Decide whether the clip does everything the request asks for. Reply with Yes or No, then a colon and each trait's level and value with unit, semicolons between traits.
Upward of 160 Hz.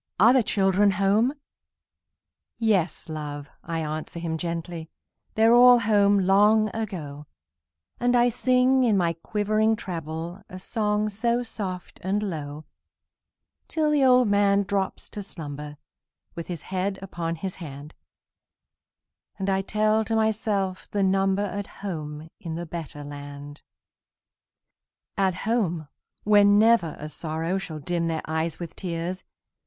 Yes: high, 190 Hz